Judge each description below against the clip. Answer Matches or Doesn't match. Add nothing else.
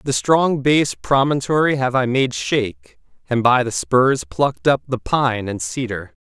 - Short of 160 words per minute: Doesn't match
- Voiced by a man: Matches